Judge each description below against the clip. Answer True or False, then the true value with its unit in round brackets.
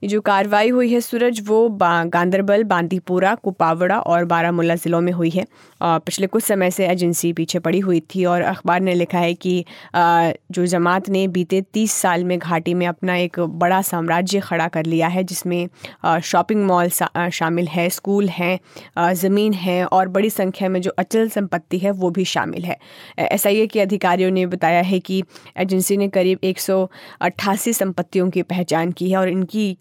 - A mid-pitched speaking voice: True (180 Hz)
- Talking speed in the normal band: True (175 wpm)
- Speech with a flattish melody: True (2.0 semitones)